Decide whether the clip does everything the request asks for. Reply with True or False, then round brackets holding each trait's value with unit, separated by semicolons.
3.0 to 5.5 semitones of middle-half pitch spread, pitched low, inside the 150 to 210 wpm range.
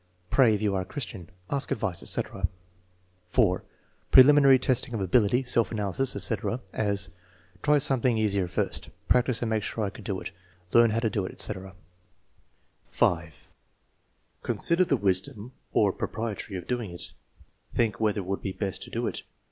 True (4.3 semitones; 110 Hz; 165 wpm)